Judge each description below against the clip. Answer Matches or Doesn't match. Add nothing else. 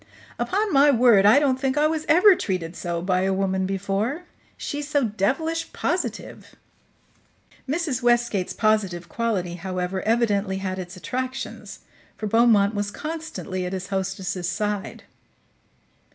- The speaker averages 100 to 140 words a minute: Matches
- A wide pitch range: Matches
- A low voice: Doesn't match